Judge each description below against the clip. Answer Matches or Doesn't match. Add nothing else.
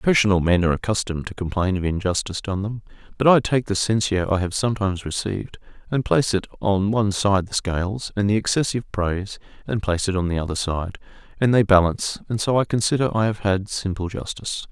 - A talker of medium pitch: Doesn't match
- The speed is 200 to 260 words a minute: Matches